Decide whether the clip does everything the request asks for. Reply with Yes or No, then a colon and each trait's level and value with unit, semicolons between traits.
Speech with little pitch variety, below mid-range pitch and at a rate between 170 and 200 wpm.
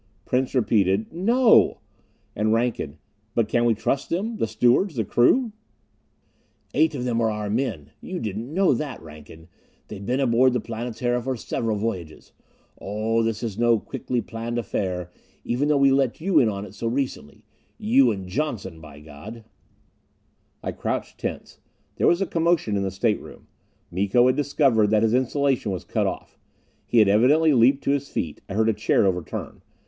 No: average, 4.5 semitones; low, 115 Hz; average, 175 wpm